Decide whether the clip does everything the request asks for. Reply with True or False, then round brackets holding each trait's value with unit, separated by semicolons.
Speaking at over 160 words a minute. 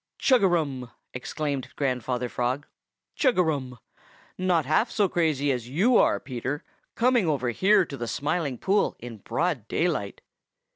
False (150 wpm)